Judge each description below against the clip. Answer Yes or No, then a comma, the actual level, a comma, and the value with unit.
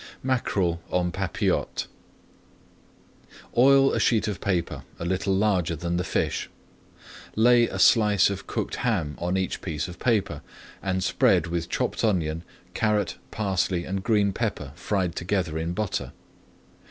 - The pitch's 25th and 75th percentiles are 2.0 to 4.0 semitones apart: Yes, average, 3.5 semitones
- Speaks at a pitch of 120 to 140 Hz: No, very low, 95 Hz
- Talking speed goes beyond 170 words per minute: No, average, 140 wpm